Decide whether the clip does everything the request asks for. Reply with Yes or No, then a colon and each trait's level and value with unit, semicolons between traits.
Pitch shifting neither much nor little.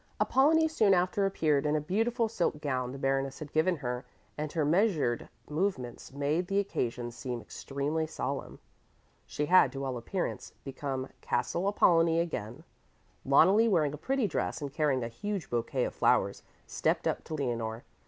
No: wide, 5.7 semitones